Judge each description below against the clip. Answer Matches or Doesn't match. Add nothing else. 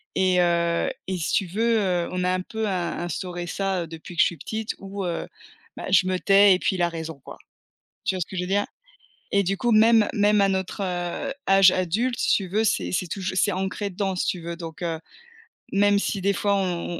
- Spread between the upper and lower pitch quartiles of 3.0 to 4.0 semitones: Doesn't match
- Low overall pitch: Doesn't match